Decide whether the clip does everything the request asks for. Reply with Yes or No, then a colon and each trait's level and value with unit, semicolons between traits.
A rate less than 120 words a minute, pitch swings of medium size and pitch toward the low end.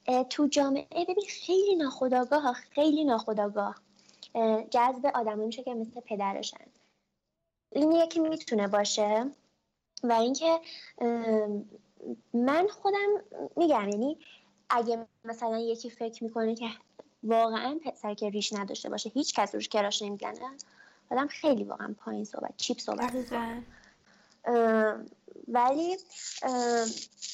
No: average, 110 wpm; average, 4.6 semitones; high, 245 Hz